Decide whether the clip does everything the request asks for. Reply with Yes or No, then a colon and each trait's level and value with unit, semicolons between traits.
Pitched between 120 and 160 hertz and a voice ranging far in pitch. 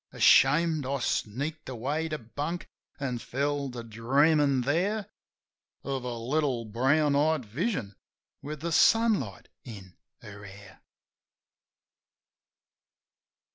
No: medium, 140 Hz; average, 4.9 semitones